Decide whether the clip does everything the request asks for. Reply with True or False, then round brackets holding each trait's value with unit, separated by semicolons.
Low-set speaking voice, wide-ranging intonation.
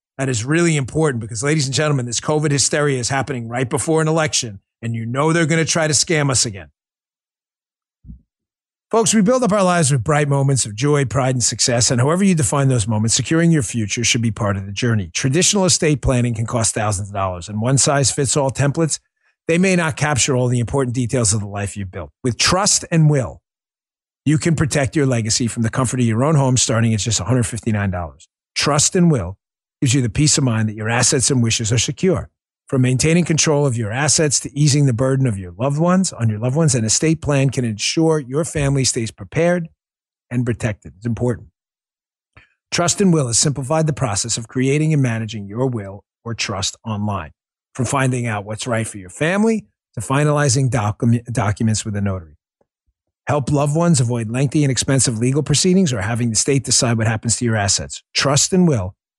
False (130 Hz; 4.7 semitones)